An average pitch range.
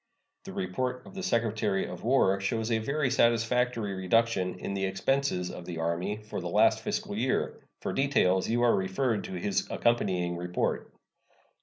Yes: average, 4.3 semitones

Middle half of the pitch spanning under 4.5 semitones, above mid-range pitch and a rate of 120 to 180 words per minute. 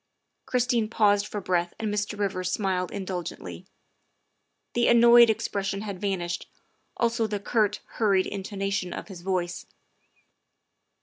Yes: average, 2.8 semitones; high, 200 Hz; slow, 135 wpm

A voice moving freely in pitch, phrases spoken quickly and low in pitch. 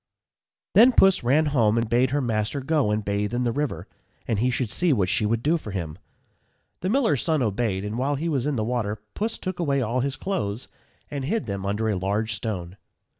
Yes: wide, 5.7 semitones; fast, 225 wpm; low, 120 Hz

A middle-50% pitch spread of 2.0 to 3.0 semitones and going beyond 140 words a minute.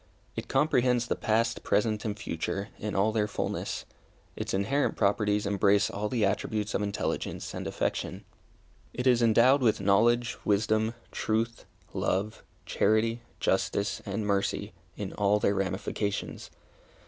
No: narrow, 2.4 semitones; slow, 135 wpm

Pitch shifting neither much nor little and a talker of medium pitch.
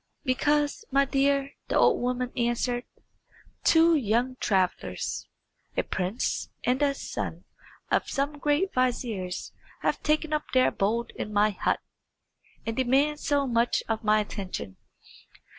No: average, 4.3 semitones; very high, 255 Hz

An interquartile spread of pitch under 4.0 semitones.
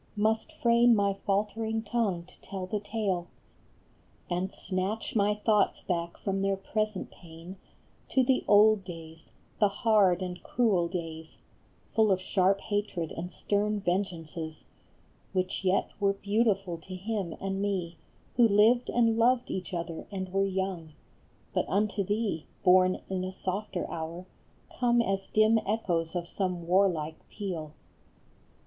Yes: average, 3.0 semitones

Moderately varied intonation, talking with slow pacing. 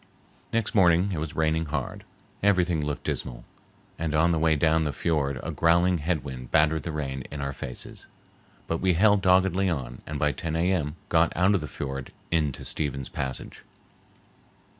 No: average, 3.3 semitones; average, 175 wpm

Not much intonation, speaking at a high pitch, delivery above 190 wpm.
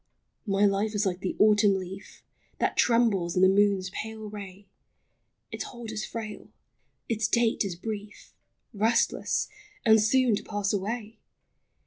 No: narrow, 2.1 semitones; high, 210 Hz; average, 150 wpm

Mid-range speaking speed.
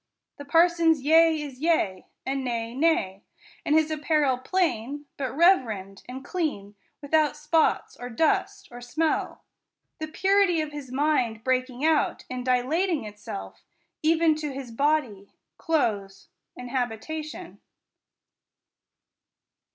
No: slow, 120 wpm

